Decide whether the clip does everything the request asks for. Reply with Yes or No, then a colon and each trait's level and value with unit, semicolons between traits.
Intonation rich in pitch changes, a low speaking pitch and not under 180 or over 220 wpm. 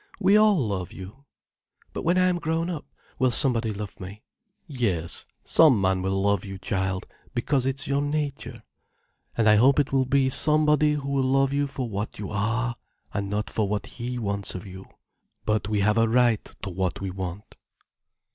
Yes: wide, 5.8 semitones; low, 115 Hz; average, 185 wpm